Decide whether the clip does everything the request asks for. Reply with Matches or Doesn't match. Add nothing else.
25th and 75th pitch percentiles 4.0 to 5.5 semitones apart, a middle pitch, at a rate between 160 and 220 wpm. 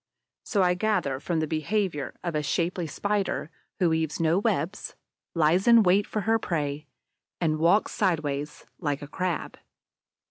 Doesn't match